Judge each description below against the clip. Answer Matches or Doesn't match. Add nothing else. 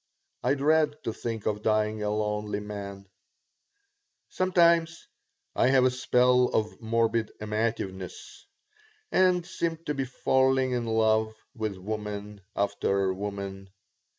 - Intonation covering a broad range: Doesn't match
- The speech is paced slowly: Matches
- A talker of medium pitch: Doesn't match